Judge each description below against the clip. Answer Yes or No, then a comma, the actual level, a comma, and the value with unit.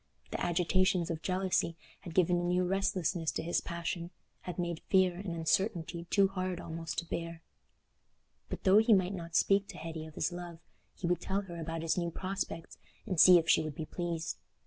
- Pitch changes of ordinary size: No, narrow, 2.0 semitones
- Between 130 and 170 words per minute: No, average, 190 wpm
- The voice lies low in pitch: No, medium, 175 Hz